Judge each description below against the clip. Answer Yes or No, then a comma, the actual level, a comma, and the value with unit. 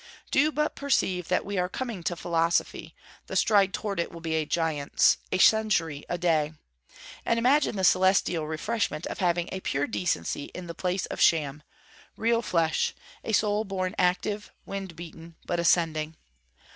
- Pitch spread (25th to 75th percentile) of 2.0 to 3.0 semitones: No, average, 4.0 semitones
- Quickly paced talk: No, average, 165 wpm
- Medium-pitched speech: Yes, medium, 180 Hz